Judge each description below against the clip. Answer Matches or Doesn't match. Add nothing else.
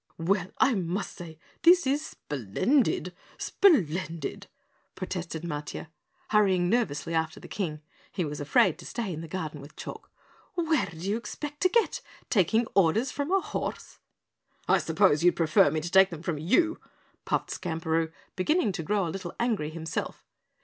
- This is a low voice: Doesn't match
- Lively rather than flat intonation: Matches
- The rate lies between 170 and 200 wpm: Doesn't match